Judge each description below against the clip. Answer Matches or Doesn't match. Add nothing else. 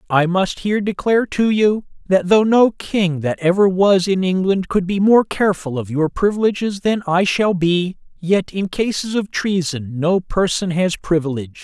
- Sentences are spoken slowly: Doesn't match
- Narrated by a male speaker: Matches